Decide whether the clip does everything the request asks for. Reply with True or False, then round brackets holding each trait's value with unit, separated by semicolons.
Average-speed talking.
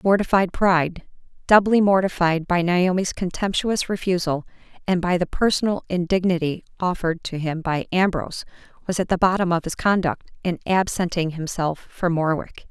False (130 wpm)